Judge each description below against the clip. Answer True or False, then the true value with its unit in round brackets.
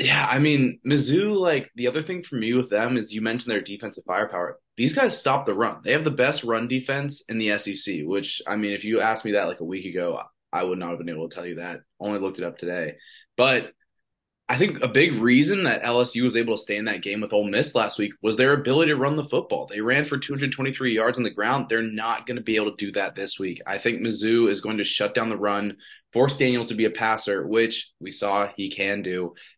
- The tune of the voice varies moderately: True (3.8 semitones)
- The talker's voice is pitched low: True (115 Hz)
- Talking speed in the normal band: False (260 wpm)